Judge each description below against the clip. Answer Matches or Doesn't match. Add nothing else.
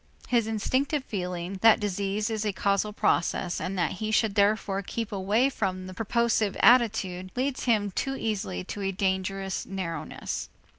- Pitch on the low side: Doesn't match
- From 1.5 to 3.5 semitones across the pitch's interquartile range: Matches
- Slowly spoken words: Doesn't match